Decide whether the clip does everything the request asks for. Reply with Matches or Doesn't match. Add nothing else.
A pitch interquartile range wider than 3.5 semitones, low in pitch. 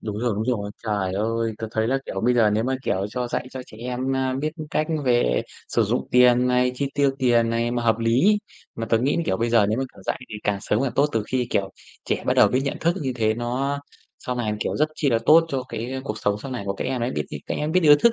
Doesn't match